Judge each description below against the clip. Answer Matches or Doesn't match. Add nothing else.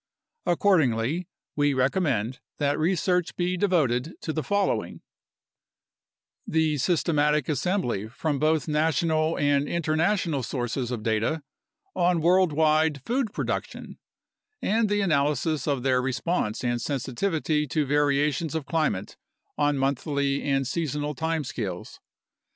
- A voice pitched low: Doesn't match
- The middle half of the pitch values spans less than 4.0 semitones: Matches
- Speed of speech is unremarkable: Doesn't match